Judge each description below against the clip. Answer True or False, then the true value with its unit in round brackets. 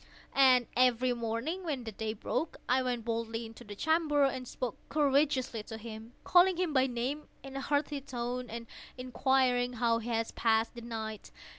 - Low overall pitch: False (245 Hz)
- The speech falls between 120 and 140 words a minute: False (175 wpm)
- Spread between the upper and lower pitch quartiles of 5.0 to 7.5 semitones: False (3.0 semitones)